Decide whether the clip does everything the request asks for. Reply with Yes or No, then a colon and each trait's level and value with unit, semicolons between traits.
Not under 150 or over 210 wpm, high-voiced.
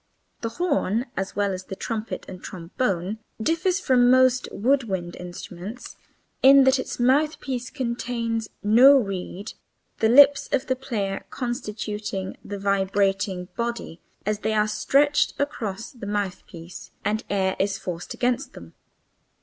No: average, 140 wpm; high, 220 Hz